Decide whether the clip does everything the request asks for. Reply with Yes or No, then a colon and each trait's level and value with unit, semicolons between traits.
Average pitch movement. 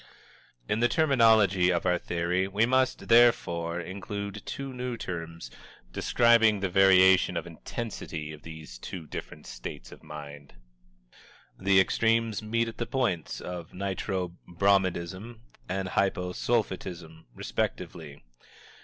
Yes: average, 4.8 semitones